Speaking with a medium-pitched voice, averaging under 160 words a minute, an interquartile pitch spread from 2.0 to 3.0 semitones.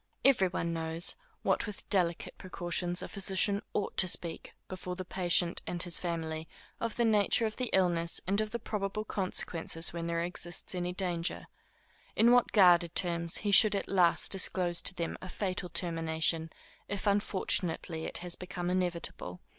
No: medium, 180 Hz; average, 165 wpm; average, 2.7 semitones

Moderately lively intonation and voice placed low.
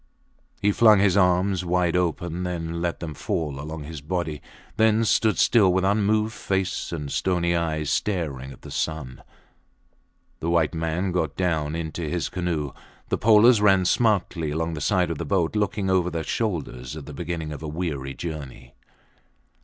Yes: average, 3.5 semitones; very low, 85 Hz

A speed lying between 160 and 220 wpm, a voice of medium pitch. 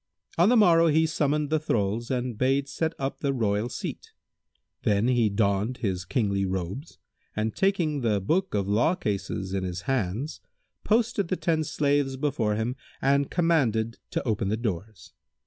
No: average, 165 wpm; low, 125 Hz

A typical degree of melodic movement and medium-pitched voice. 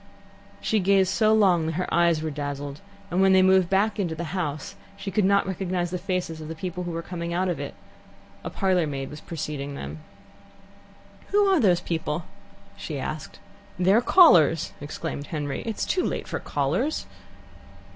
Yes: average, 3.5 semitones; medium, 175 Hz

